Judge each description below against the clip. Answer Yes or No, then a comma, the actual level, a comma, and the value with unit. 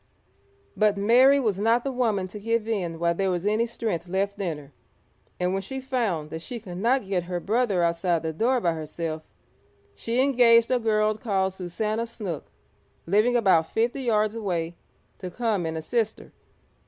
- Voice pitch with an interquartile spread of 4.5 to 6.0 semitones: Yes, average, 4.9 semitones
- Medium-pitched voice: No, high, 205 Hz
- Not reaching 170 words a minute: No, average, 180 wpm